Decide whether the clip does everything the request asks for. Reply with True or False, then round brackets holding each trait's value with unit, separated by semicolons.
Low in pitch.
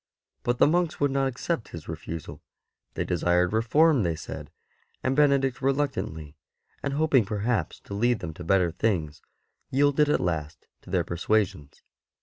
True (110 Hz)